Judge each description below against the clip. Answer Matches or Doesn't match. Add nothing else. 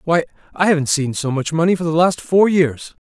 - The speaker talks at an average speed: Doesn't match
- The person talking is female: Doesn't match